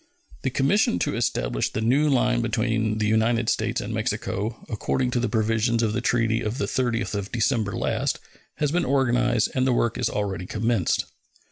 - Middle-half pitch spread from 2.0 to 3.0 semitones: Yes, narrow, 2.4 semitones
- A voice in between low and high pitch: No, low, 115 Hz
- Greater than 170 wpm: Yes, average, 180 wpm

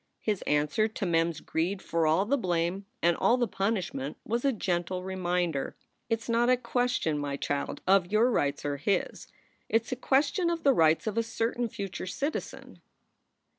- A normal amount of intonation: No, wide, 5.8 semitones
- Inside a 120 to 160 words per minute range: No, average, 185 wpm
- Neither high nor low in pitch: No, high, 195 Hz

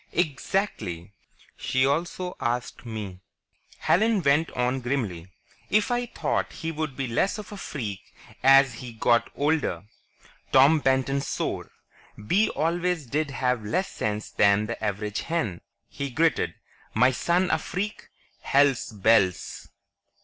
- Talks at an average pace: No, slow, 125 wpm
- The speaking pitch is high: No, low, 135 Hz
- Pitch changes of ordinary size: No, wide, 6.6 semitones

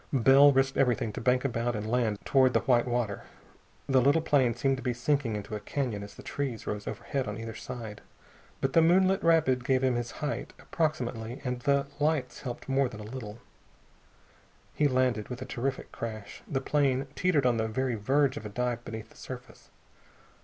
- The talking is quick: No, average, 195 wpm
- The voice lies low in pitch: Yes, low, 125 Hz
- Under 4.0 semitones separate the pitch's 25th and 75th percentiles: Yes, average, 3.1 semitones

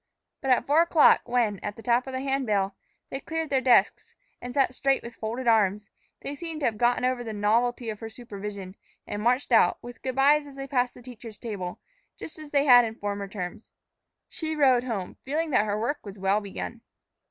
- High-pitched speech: Yes, high, 240 Hz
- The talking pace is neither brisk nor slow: No, fast, 215 wpm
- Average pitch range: Yes, average, 4.3 semitones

